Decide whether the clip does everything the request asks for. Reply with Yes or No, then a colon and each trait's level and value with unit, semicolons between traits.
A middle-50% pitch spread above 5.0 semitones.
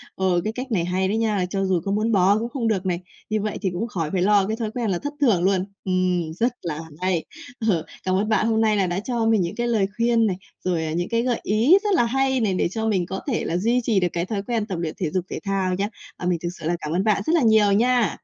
No: average, 3.8 semitones